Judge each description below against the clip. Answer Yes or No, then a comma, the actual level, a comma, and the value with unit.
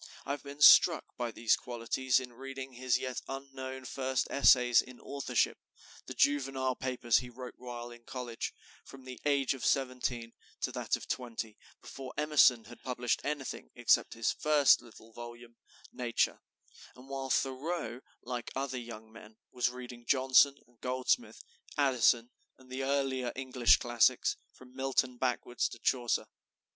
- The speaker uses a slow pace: No, average, 150 wpm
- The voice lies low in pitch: Yes, low, 130 Hz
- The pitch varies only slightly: Yes, narrow, 1.9 semitones